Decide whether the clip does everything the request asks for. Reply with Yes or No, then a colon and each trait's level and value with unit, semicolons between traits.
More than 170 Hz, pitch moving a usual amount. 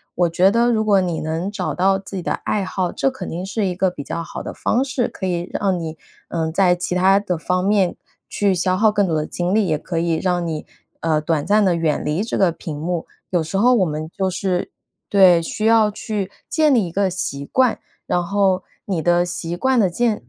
Yes: medium, 185 Hz; average, 3.1 semitones